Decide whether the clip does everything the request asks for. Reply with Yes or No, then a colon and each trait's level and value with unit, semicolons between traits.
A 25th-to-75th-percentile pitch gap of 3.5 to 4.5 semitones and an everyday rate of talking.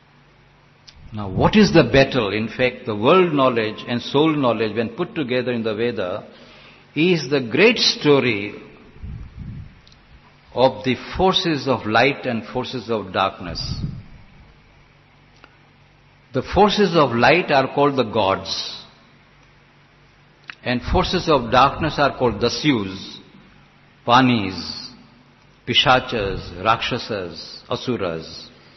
Yes: average, 4.1 semitones; average, 105 wpm